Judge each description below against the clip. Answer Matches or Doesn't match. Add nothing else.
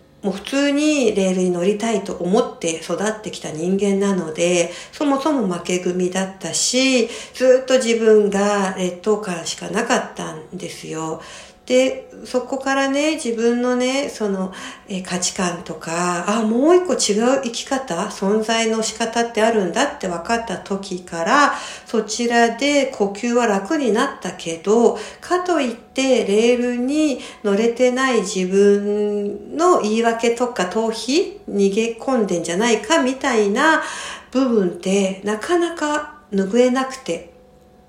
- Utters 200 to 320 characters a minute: Matches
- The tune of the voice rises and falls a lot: Doesn't match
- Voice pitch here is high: Matches